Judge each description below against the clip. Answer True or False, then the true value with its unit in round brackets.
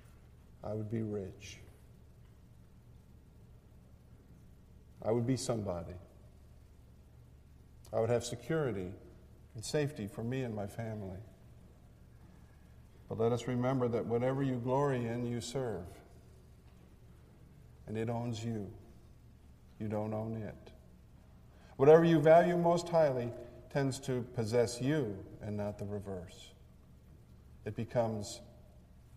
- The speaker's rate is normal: False (110 wpm)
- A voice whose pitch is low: True (100 Hz)